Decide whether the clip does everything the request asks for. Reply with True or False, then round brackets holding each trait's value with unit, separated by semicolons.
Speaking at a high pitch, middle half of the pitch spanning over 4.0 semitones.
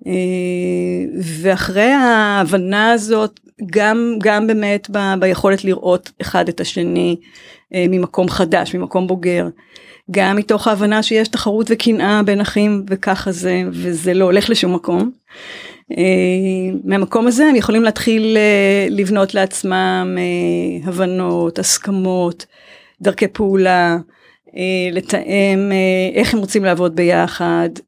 False (195 Hz; 2.6 semitones)